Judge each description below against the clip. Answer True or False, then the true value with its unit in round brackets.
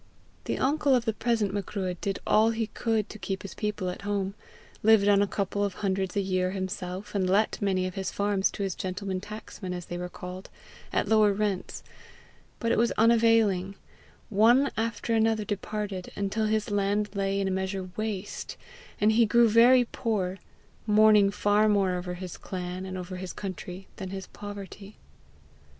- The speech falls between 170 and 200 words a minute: True (175 wpm)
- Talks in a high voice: True (200 Hz)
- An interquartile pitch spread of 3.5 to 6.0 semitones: False (2.4 semitones)